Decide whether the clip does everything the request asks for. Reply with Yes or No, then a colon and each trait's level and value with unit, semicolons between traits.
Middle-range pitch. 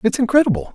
No: high, 215 Hz